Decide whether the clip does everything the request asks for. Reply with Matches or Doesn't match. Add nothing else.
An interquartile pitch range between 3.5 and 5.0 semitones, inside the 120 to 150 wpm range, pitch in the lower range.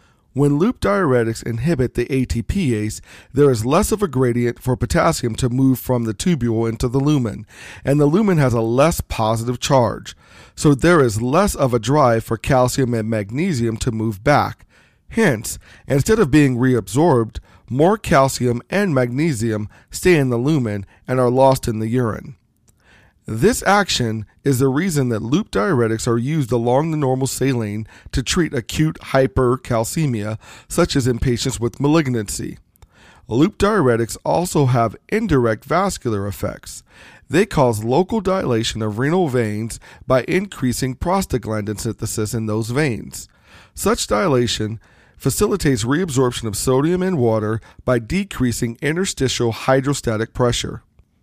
Matches